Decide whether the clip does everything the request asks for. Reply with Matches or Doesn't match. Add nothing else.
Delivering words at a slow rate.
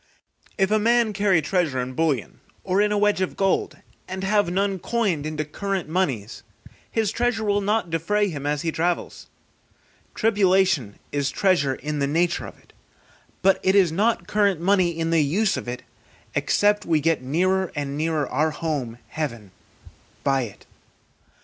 Doesn't match